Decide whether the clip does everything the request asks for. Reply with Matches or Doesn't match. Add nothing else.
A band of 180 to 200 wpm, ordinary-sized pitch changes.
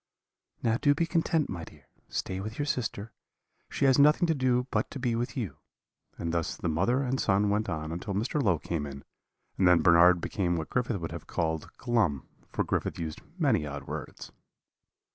Doesn't match